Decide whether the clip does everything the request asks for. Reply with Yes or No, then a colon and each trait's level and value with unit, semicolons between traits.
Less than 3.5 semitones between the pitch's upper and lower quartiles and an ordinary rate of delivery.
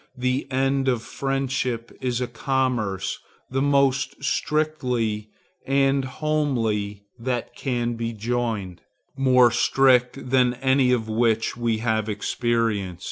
No: average, 2.8 semitones; slow, 115 wpm